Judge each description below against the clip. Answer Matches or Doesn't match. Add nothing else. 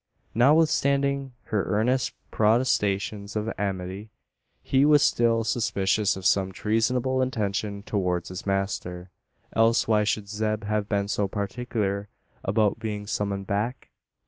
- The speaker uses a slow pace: Matches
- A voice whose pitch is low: Matches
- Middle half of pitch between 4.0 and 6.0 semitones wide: Doesn't match